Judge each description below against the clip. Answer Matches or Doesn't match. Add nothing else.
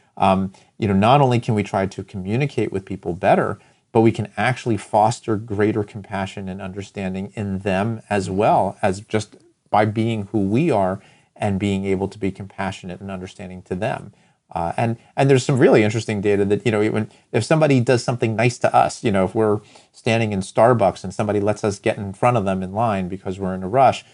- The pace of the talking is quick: Matches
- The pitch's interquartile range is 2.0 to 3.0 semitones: Matches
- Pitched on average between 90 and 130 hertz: Matches